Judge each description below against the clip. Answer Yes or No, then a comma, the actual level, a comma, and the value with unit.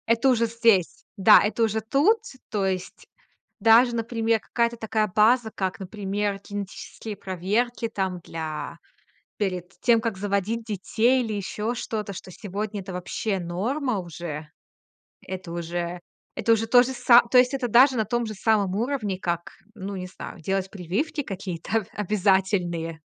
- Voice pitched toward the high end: Yes, high, 210 Hz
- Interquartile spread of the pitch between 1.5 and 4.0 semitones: Yes, average, 3.7 semitones